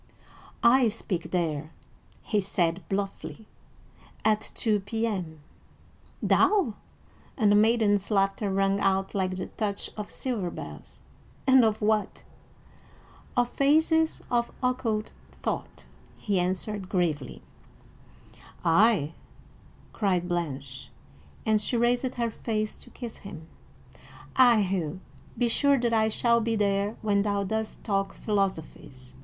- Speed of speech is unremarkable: No, slow, 120 wpm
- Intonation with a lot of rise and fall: No, average, 3.5 semitones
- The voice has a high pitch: Yes, high, 210 Hz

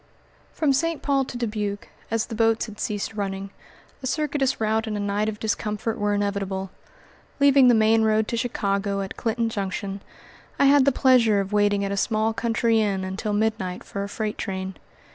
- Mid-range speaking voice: No, high, 215 Hz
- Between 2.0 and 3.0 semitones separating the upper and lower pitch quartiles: Yes, narrow, 2.5 semitones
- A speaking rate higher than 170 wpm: Yes, average, 185 wpm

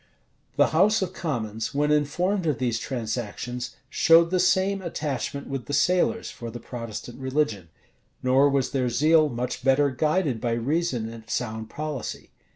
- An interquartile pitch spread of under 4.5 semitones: No, average, 5.0 semitones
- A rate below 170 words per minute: Yes, average, 155 wpm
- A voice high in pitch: No, low, 135 Hz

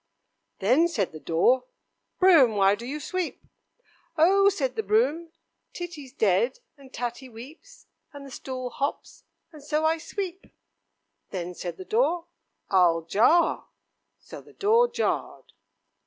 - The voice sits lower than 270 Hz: No, very high, 280 Hz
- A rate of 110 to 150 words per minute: Yes, slow, 135 wpm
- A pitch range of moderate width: No, wide, 7.1 semitones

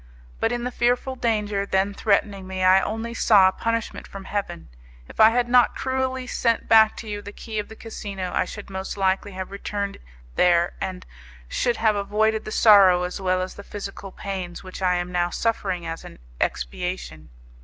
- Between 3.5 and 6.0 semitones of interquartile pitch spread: No, average, 3.0 semitones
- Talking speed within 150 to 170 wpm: No, average, 190 wpm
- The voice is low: No, high, 200 Hz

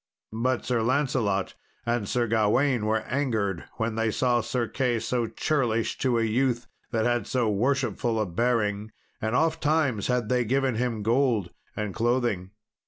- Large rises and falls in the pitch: No, narrow, 2.6 semitones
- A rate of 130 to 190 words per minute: Yes, average, 155 wpm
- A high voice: No, low, 120 Hz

